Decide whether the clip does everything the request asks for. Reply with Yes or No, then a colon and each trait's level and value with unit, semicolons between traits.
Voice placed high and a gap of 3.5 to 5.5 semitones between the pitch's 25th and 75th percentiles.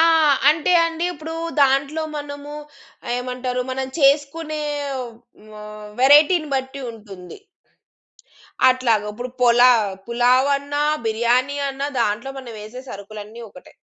Yes: very high, 255 Hz; average, 3.8 semitones